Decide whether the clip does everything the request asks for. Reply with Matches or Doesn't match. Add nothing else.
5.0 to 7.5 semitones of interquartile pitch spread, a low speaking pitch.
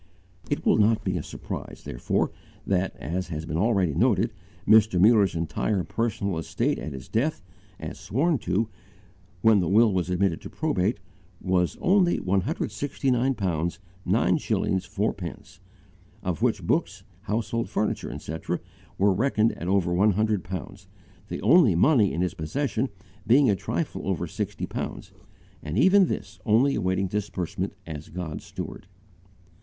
Doesn't match